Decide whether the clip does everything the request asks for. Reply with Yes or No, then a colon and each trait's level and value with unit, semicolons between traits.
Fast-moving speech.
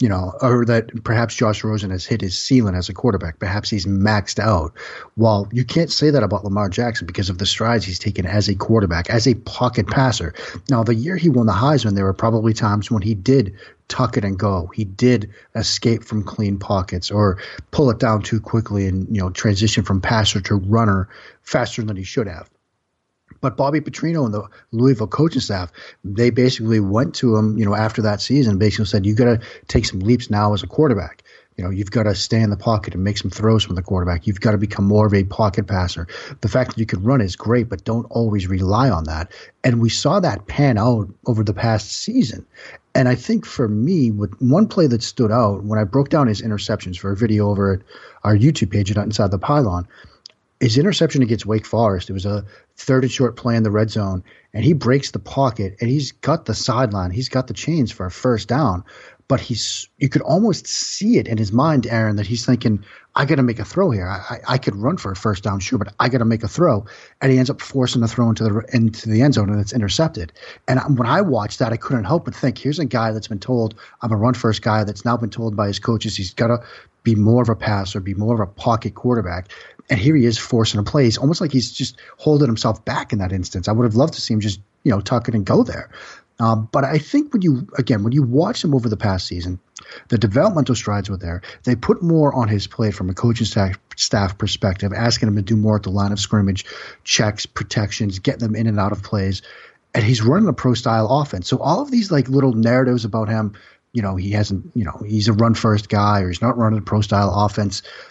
Yes: fast, 245 wpm